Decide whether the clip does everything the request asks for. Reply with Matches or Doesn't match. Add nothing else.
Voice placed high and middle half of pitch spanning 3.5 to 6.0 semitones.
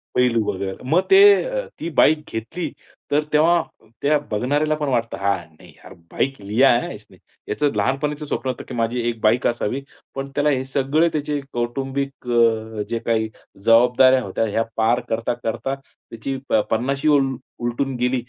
Doesn't match